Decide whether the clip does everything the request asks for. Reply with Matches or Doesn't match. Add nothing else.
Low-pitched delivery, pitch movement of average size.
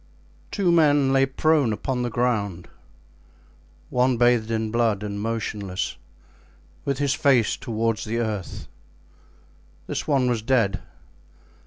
Matches